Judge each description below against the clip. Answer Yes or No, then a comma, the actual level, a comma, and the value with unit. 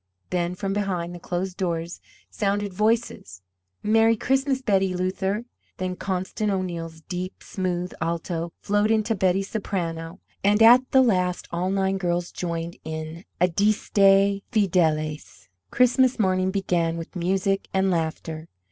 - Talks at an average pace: No, slow, 130 wpm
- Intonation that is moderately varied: Yes, average, 3.0 semitones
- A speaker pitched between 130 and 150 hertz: No, medium, 185 Hz